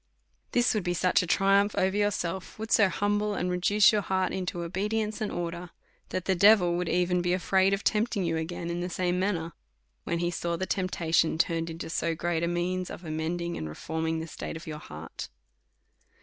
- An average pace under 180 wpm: No, fast, 205 wpm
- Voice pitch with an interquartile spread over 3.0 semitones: No, average, 2.7 semitones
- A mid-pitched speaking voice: Yes, medium, 180 Hz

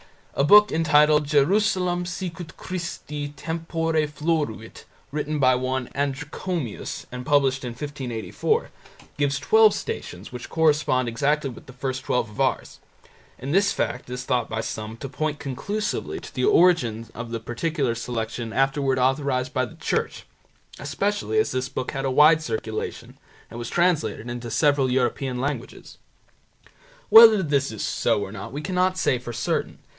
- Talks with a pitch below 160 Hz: Yes, medium, 140 Hz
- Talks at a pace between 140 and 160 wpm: Yes, average, 150 wpm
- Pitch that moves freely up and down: No, average, 4.5 semitones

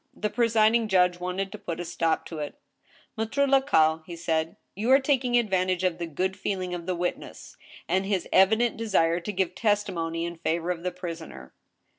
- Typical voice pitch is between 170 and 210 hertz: Yes, medium, 185 Hz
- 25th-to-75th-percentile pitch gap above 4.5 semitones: No, average, 4.1 semitones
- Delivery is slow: No, average, 195 wpm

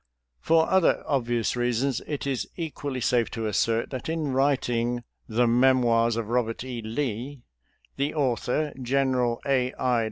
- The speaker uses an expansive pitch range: No, average, 2.8 semitones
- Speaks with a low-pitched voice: Yes, low, 125 Hz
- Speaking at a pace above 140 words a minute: Yes, average, 155 wpm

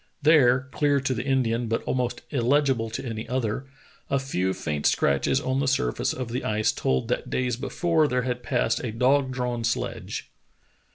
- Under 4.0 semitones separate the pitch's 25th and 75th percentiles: Yes, average, 2.7 semitones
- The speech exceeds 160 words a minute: Yes, average, 175 wpm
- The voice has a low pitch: Yes, low, 125 Hz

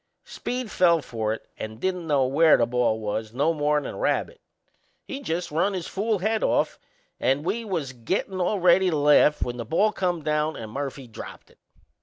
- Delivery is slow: No, average, 195 wpm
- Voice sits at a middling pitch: Yes, medium, 155 Hz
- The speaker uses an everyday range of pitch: No, wide, 6.4 semitones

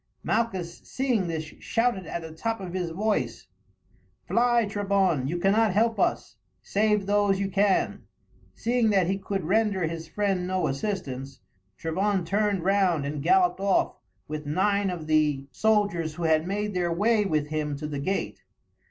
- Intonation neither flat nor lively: Yes, average, 4.2 semitones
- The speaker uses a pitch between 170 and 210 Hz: Yes, high, 190 Hz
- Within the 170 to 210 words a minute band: No, average, 160 wpm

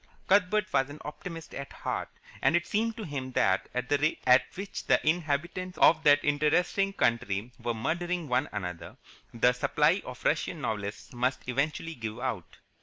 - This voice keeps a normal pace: Yes, average, 170 wpm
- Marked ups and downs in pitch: Yes, wide, 5.8 semitones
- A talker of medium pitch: Yes, medium, 145 Hz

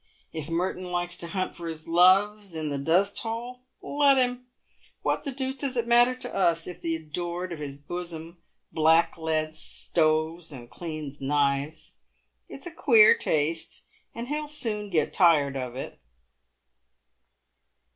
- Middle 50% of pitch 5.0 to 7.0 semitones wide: Yes, average, 5.3 semitones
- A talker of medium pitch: Yes, medium, 170 Hz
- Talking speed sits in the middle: Yes, average, 145 wpm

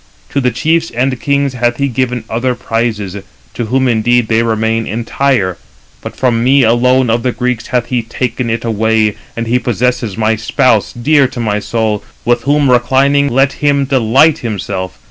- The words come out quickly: No, average, 175 wpm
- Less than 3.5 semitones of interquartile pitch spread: Yes, narrow, 2.6 semitones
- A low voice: Yes, low, 120 Hz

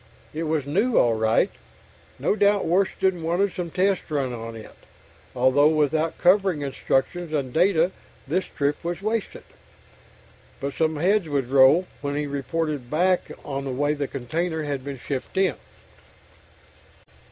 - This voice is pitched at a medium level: Yes, medium, 155 Hz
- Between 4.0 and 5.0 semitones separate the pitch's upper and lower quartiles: Yes, average, 4.5 semitones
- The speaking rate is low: No, average, 145 wpm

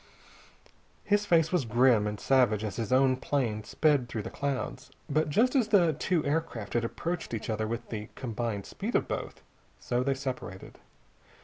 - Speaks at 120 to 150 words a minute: No, average, 175 wpm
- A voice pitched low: Yes, low, 130 Hz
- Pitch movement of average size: No, wide, 5.8 semitones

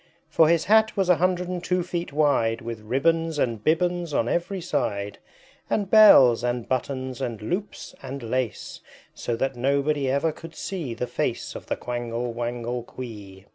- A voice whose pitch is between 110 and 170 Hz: Yes, low, 135 Hz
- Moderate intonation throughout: No, wide, 6.2 semitones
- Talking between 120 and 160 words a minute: No, average, 170 wpm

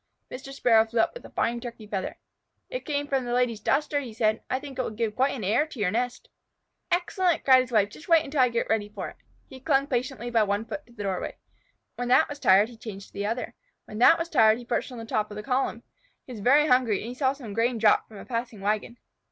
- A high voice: Yes, high, 240 Hz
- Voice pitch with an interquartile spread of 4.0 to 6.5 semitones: No, average, 3.6 semitones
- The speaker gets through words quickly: Yes, fast, 260 wpm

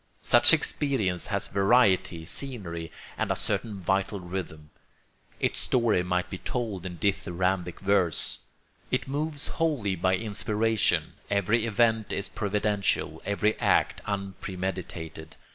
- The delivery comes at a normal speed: No, slow, 115 wpm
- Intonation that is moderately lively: Yes, average, 3.3 semitones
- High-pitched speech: No, low, 100 Hz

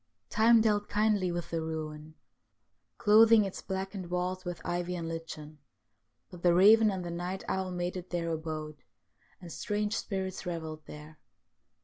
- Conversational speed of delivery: Yes, average, 150 wpm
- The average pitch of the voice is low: No, medium, 180 Hz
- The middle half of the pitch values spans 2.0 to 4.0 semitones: Yes, average, 3.2 semitones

